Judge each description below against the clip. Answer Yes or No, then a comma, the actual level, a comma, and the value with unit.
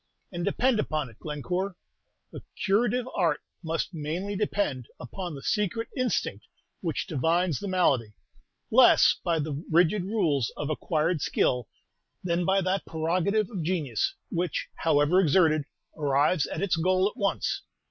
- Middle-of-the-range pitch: Yes, medium, 170 Hz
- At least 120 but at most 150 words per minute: Yes, average, 140 wpm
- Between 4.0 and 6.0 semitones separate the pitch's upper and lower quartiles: Yes, average, 4.3 semitones